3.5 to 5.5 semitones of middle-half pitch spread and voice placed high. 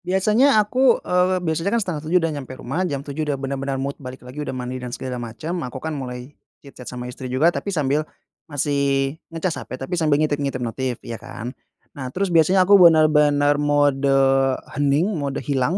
No: average, 3.9 semitones; medium, 145 Hz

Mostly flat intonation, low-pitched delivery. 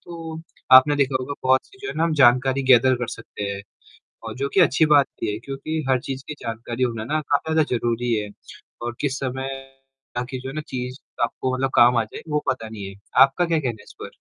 No: average, 3.1 semitones; low, 130 Hz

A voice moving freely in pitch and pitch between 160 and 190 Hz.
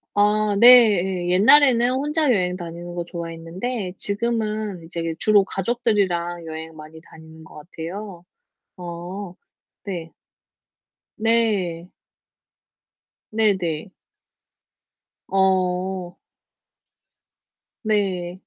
No: average, 3.7 semitones; medium, 185 Hz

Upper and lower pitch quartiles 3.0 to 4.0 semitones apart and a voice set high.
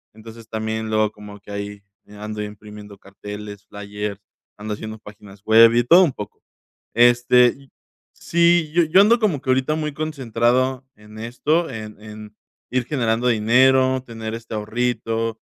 No: average, 3.5 semitones; low, 115 Hz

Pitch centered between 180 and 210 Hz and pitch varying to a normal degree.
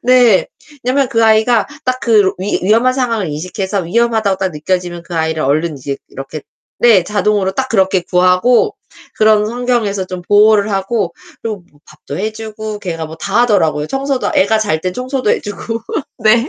Yes: high, 205 Hz; average, 4.1 semitones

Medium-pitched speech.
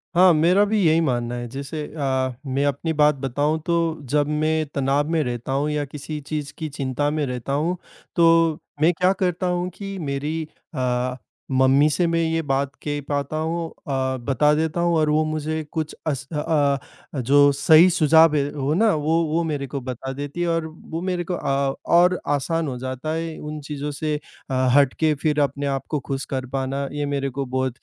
Yes: medium, 150 Hz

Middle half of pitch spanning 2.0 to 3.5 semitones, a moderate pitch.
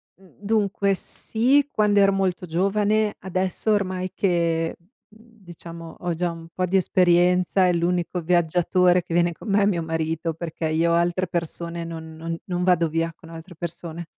Yes: narrow, 2.5 semitones; medium, 175 Hz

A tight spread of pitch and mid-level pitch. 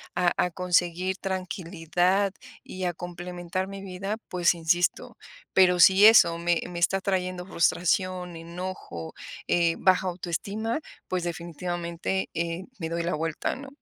Yes: narrow, 1.7 semitones; medium, 180 Hz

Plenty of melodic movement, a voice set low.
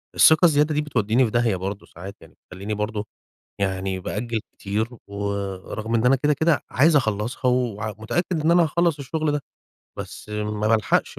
Yes: wide, 6.2 semitones; low, 115 Hz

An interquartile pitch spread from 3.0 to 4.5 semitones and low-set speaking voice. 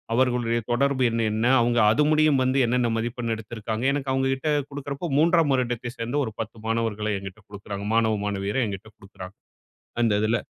Yes: average, 3.5 semitones; low, 115 Hz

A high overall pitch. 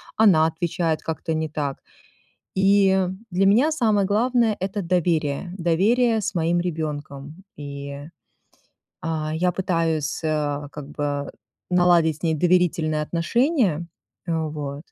No: medium, 165 Hz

